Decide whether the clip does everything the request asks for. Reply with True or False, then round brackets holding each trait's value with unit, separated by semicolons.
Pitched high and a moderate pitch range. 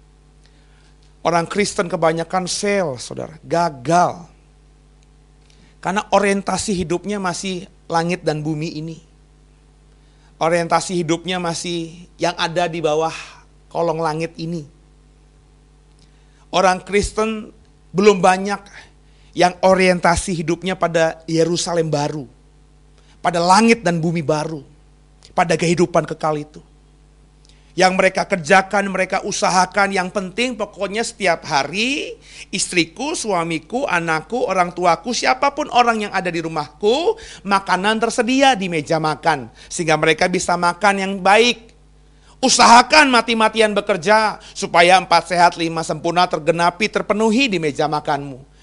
False (170 Hz; 4.5 semitones)